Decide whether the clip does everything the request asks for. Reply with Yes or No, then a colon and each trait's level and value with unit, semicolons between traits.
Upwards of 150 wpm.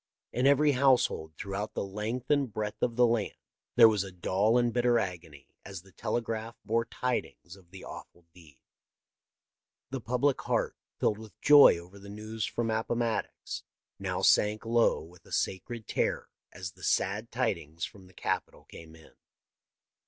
Yes: average, 160 wpm